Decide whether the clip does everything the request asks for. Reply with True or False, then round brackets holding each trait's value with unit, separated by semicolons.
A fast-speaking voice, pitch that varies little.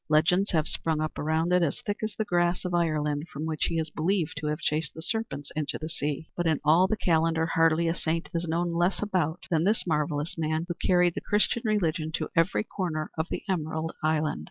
True (225 wpm; 2.3 semitones)